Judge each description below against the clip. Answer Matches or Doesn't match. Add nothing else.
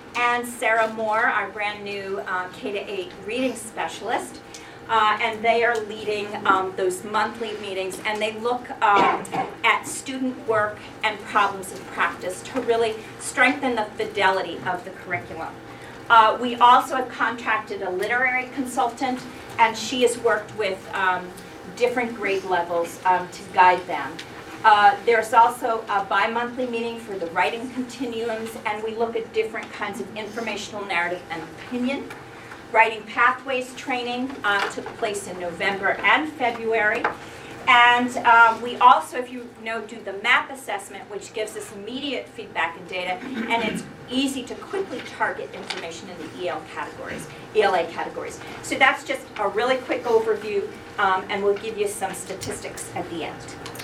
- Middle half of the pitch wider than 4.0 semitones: Doesn't match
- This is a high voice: Matches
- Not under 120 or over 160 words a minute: Matches